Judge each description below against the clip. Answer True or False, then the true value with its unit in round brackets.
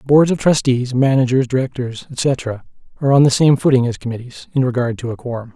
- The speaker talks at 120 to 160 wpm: False (195 wpm)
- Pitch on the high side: False (130 Hz)